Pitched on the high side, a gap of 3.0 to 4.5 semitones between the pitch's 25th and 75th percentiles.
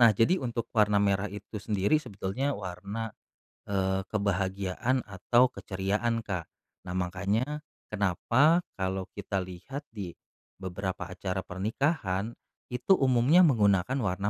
No: low, 100 Hz; average, 3.9 semitones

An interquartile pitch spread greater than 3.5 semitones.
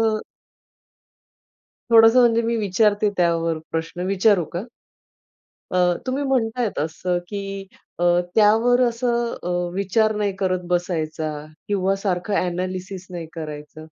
Yes: average, 4.2 semitones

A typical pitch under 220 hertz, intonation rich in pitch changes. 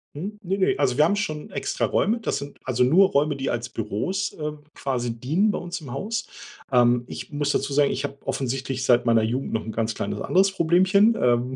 Yes: medium, 140 Hz; wide, 7.3 semitones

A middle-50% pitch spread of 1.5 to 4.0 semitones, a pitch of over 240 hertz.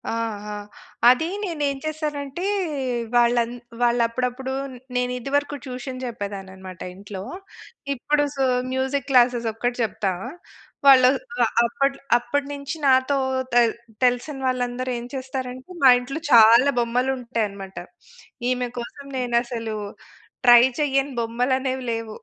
Yes: narrow, 2.5 semitones; very high, 250 Hz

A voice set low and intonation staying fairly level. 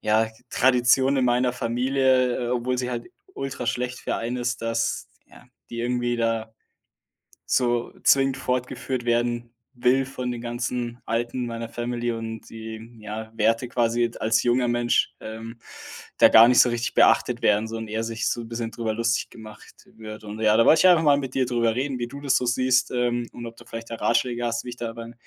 Yes: low, 120 Hz; narrow, 1.5 semitones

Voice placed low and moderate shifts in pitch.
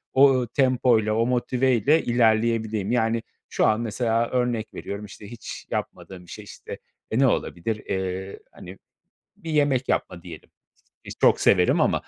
Yes: low, 115 Hz; average, 3.3 semitones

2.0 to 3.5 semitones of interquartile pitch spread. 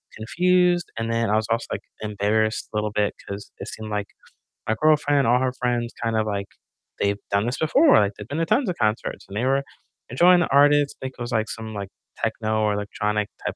No: average, 4.8 semitones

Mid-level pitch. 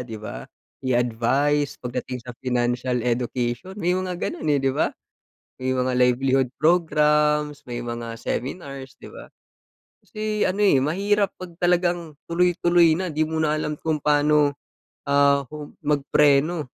Yes: medium, 145 Hz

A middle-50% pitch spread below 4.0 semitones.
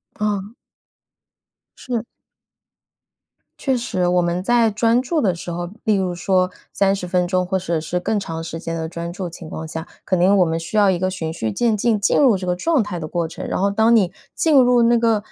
No: average, 4.3 semitones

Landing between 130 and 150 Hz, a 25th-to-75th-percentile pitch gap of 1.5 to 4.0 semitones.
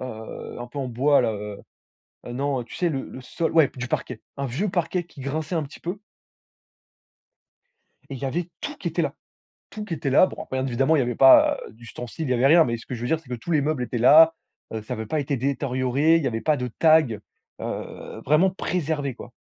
No: medium, 140 Hz; average, 4.4 semitones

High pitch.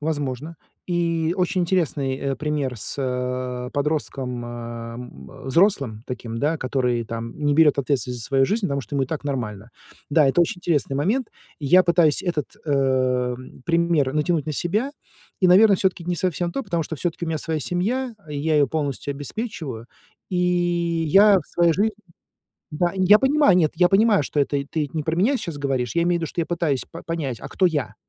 No: medium, 155 Hz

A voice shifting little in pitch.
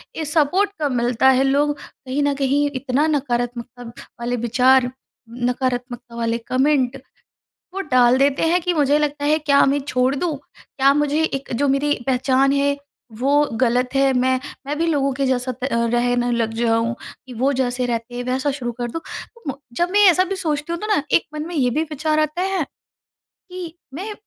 No: average, 3.2 semitones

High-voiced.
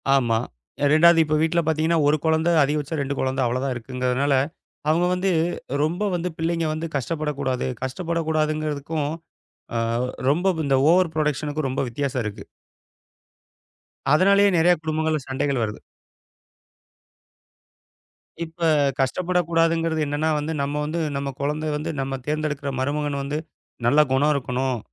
No: medium, 150 Hz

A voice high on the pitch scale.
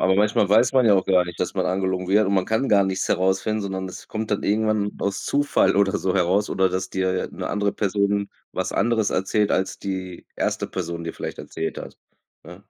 No: low, 100 Hz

